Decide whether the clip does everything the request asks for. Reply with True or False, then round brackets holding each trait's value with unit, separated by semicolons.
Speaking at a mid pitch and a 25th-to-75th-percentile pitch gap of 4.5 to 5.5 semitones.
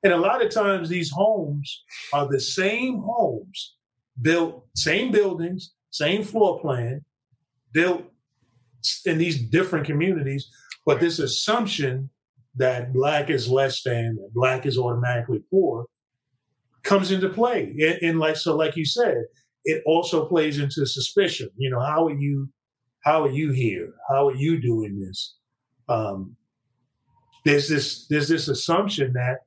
True (145 Hz; 4.9 semitones)